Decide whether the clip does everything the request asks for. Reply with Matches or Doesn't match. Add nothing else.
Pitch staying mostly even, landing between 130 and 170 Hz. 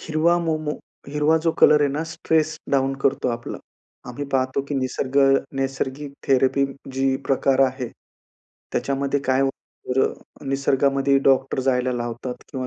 Matches